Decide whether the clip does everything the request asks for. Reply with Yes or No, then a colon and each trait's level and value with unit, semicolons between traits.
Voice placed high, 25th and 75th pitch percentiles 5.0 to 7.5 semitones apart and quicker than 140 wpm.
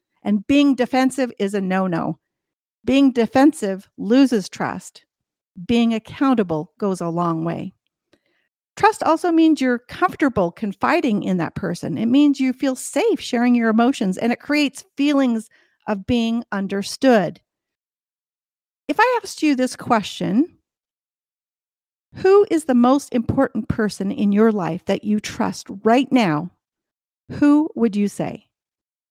No: high, 235 Hz; average, 5.3 semitones; slow, 135 wpm